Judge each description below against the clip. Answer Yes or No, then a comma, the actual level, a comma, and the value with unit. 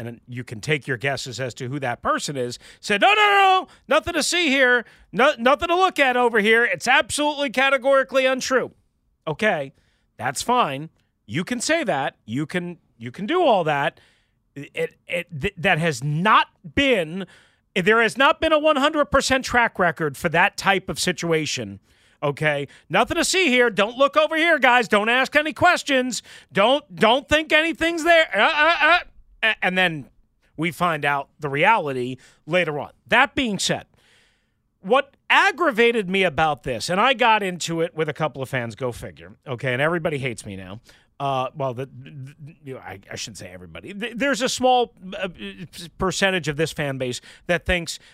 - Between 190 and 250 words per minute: No, average, 180 wpm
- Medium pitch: Yes, medium, 180 Hz